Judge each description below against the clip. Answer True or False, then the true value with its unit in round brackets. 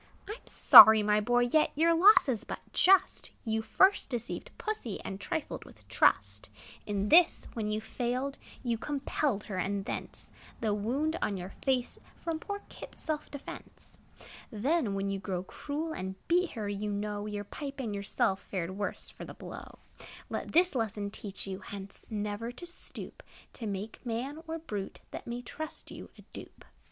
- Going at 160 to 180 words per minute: True (175 wpm)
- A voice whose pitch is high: True (225 Hz)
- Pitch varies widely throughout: True (6.5 semitones)